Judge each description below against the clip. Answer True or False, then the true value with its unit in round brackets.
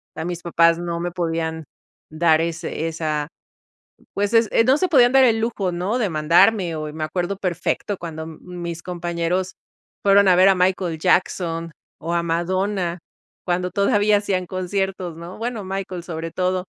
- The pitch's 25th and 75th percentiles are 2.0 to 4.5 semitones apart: True (2.7 semitones)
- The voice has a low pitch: False (180 Hz)